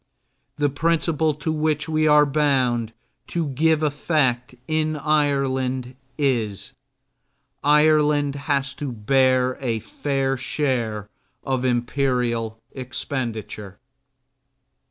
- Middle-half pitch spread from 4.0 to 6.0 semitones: No, average, 3.1 semitones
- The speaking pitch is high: No, low, 135 Hz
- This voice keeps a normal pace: No, slow, 95 wpm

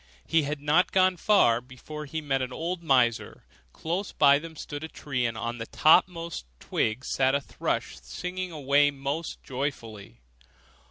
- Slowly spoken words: No, average, 160 wpm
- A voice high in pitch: No, medium, 145 Hz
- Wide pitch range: No, average, 4.4 semitones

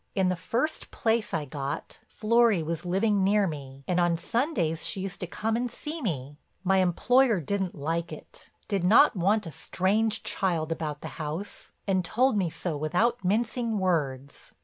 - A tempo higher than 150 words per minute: Yes, average, 170 wpm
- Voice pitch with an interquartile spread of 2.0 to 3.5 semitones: No, average, 5.3 semitones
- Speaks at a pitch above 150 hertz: Yes, medium, 185 Hz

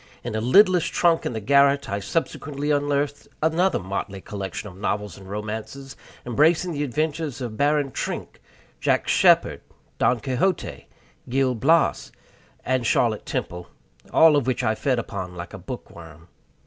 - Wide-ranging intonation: Yes, wide, 6.0 semitones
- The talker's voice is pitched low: Yes, low, 130 Hz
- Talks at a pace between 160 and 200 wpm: No, average, 150 wpm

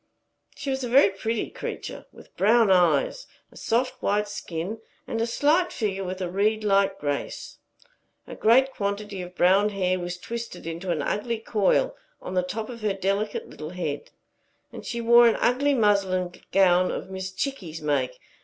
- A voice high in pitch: Yes, high, 200 Hz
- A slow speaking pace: No, average, 170 wpm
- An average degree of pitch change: Yes, average, 4.1 semitones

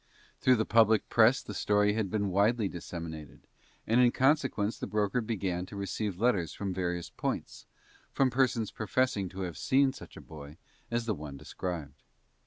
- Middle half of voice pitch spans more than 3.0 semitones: Yes, average, 4.6 semitones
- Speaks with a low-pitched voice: Yes, low, 105 Hz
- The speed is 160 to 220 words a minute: Yes, average, 170 wpm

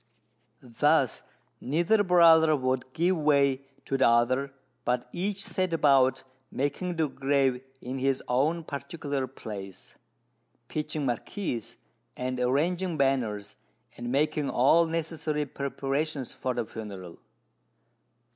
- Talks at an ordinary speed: No, slow, 110 wpm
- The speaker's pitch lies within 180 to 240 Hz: No, medium, 140 Hz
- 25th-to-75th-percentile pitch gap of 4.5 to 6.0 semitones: No, average, 3.9 semitones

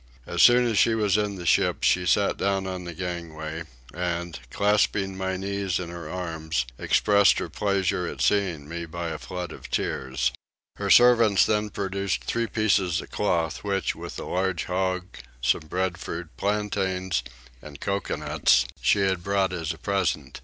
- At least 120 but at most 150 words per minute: No, average, 165 wpm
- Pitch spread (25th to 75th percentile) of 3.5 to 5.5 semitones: No, average, 2.9 semitones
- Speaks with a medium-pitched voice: No, very low, 95 Hz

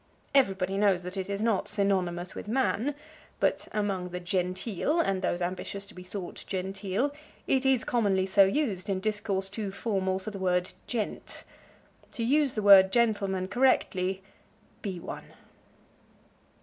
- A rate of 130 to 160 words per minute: Yes, average, 150 wpm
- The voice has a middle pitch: No, high, 195 Hz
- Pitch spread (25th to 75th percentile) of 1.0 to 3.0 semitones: Yes, average, 2.7 semitones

